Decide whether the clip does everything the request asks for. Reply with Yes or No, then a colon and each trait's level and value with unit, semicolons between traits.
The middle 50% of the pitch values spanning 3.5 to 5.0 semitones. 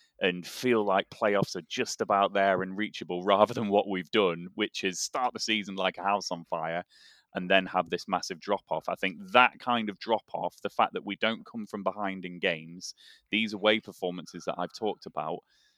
No: narrow, 2.6 semitones